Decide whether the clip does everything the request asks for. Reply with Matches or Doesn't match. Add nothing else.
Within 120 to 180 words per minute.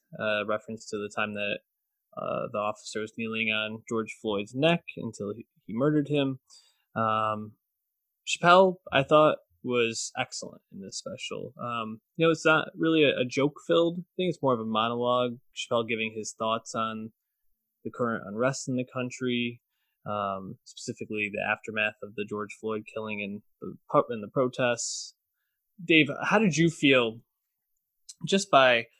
Matches